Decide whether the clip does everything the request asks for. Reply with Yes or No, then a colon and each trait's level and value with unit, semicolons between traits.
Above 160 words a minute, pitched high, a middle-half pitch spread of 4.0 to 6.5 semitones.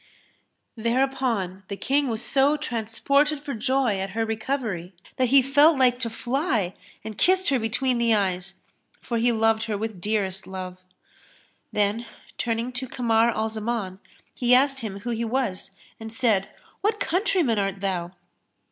No: average, 155 wpm; high, 230 Hz; average, 4.3 semitones